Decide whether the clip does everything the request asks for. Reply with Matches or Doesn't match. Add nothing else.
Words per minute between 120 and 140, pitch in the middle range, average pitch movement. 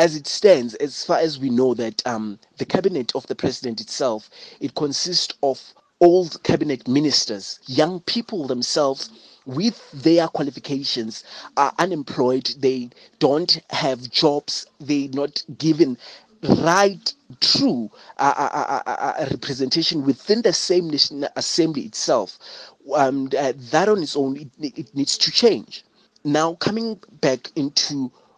Matches